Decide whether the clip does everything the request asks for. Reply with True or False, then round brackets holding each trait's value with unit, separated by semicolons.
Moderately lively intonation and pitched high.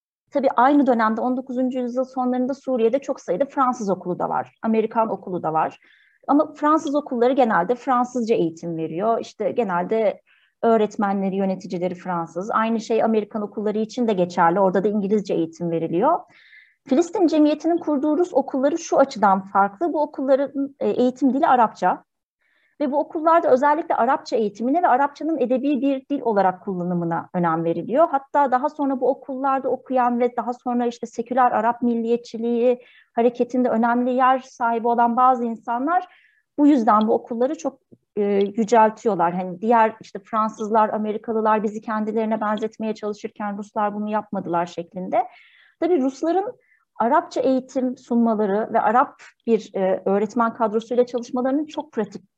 True (4.2 semitones; 235 Hz)